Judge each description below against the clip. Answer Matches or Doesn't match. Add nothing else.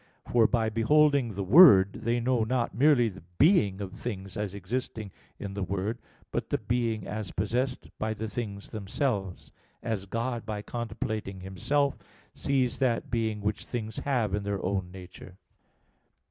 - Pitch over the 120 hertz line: Doesn't match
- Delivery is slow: Doesn't match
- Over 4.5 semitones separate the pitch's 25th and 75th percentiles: Doesn't match